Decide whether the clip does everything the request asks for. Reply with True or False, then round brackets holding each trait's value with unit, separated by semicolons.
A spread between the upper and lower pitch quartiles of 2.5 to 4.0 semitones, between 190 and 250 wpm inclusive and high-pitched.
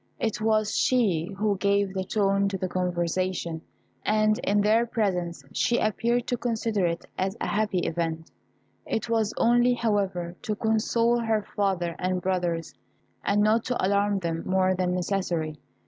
False (3.3 semitones; 155 wpm; 200 Hz)